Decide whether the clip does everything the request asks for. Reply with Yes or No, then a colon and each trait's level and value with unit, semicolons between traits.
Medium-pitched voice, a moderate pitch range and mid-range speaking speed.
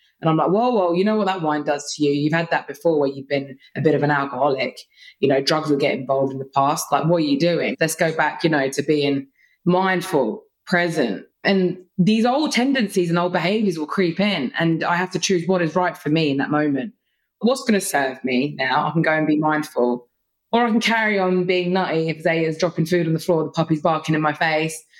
No: medium, 160 Hz; average, 4.0 semitones; fast, 245 wpm